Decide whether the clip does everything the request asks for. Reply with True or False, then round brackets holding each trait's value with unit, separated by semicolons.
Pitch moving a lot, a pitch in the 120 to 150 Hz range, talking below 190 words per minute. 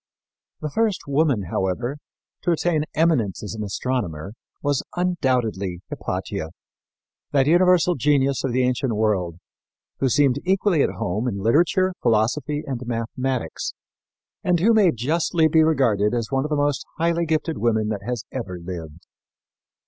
True (6.5 semitones; 135 Hz; 145 wpm)